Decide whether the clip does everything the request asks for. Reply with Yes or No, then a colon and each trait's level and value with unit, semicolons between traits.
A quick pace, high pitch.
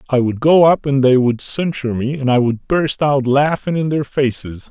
No: fast, 230 wpm; low, 135 Hz